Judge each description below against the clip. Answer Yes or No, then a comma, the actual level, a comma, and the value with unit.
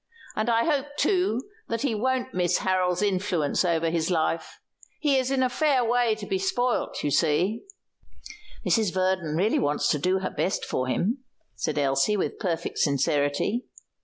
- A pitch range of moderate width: No, wide, 6.5 semitones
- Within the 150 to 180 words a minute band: Yes, average, 160 wpm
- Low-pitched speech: No, high, 190 Hz